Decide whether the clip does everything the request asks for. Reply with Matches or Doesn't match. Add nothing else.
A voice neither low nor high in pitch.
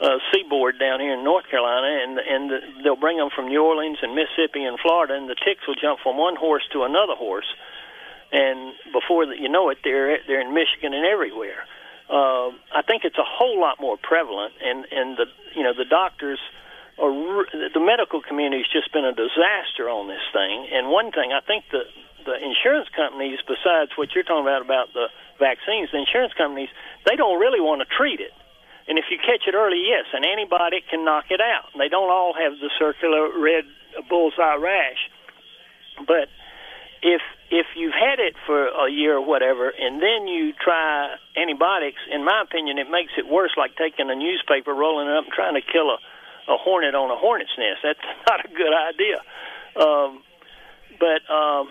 Matches